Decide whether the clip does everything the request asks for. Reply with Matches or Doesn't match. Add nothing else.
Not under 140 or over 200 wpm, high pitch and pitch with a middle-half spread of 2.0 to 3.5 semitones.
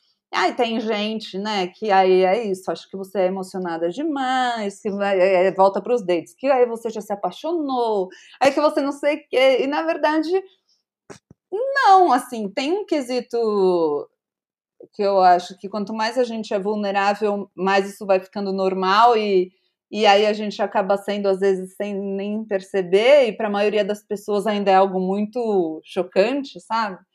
Doesn't match